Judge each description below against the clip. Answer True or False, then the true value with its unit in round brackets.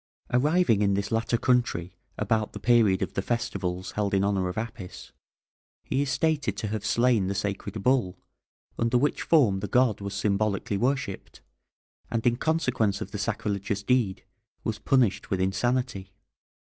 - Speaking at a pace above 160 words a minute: False (155 wpm)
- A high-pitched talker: False (110 Hz)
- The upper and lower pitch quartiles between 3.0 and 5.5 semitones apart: True (4.0 semitones)